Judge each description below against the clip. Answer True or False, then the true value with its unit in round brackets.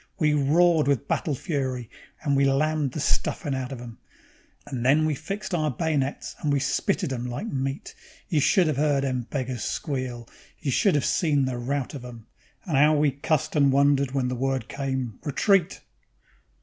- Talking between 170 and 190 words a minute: True (185 wpm)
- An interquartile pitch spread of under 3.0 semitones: True (2.6 semitones)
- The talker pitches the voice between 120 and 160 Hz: True (140 Hz)